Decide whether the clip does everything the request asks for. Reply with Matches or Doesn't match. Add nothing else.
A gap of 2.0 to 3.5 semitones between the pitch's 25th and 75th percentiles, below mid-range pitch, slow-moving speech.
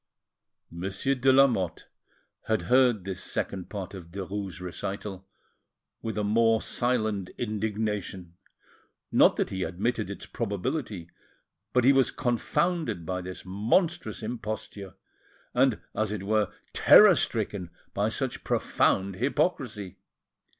Doesn't match